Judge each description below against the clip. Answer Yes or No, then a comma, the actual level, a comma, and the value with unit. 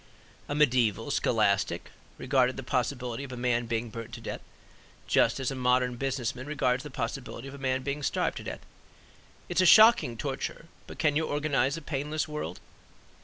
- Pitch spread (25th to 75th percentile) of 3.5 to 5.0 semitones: No, average, 2.9 semitones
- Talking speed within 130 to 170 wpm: No, average, 185 wpm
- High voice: No, low, 130 Hz